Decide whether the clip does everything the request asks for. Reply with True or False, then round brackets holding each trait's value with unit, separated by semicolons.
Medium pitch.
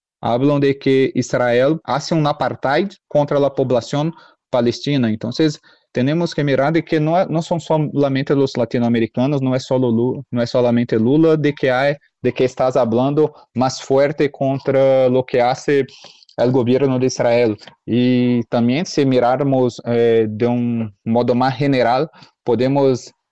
False (130 Hz)